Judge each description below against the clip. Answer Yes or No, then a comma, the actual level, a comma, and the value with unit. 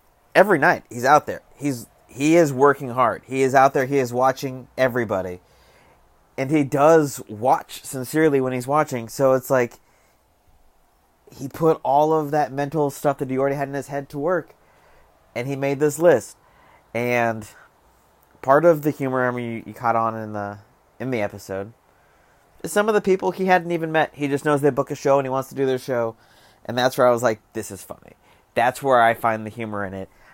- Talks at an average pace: No, fast, 210 wpm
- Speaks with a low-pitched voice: Yes, low, 130 Hz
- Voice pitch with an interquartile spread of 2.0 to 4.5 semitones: Yes, average, 4.1 semitones